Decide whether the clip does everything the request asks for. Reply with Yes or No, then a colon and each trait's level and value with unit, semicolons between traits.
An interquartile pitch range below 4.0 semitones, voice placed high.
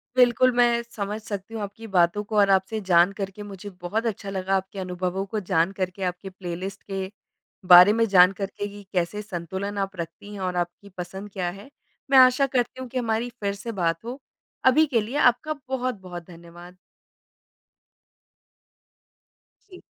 Yes: average, 3.6 semitones; high, 200 Hz